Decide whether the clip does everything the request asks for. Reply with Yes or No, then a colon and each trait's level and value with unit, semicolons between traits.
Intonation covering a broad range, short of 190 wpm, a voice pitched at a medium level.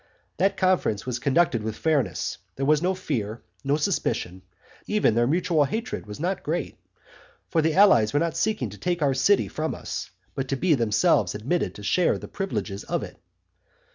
Yes: wide, 7.3 semitones; average, 180 wpm; medium, 150 Hz